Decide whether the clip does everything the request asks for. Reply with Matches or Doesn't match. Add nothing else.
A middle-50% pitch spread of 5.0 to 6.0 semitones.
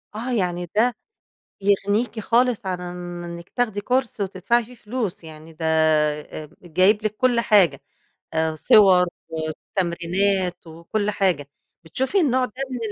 Matches